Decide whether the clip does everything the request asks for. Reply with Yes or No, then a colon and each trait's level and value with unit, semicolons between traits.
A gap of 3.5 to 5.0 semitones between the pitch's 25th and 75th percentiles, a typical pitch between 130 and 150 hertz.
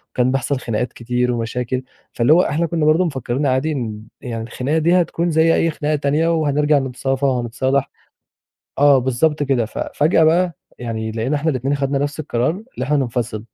Yes: average, 3.8 semitones; low, 135 Hz